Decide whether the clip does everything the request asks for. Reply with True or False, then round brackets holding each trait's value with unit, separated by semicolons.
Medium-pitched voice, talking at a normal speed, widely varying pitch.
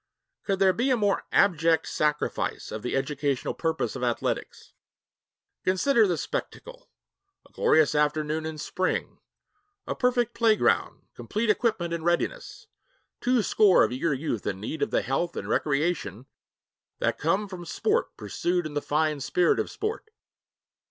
True (170 Hz; 145 wpm; 6.0 semitones)